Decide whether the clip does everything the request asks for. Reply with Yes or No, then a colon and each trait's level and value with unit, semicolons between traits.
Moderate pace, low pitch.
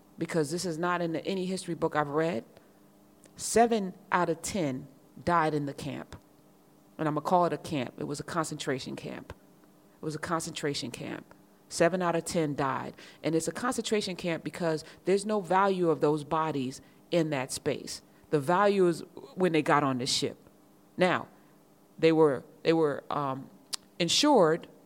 No: average, 170 wpm; medium, 160 Hz